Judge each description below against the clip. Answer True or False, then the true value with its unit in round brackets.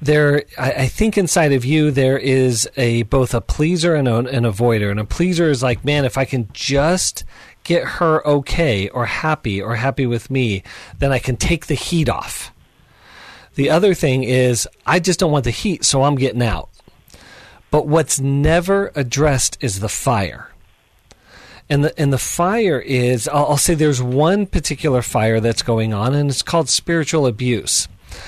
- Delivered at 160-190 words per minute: True (175 wpm)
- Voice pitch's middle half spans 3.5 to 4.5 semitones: True (4.2 semitones)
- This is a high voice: False (135 Hz)